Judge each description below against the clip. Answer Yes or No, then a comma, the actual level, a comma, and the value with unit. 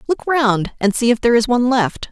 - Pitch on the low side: No, high, 240 Hz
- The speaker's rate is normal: No, fast, 255 wpm